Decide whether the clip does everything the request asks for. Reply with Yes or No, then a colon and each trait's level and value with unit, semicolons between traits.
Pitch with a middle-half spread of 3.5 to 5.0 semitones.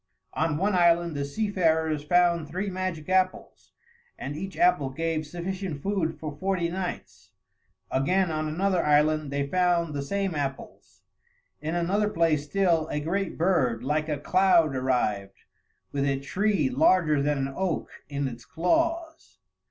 Yes: average, 4.2 semitones